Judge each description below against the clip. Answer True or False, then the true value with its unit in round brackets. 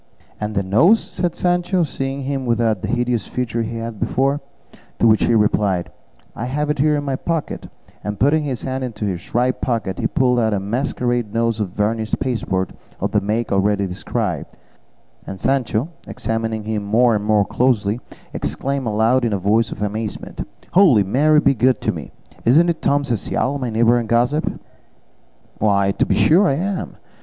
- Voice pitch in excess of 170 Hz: False (120 Hz)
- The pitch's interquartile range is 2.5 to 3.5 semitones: False (4.3 semitones)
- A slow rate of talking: False (180 wpm)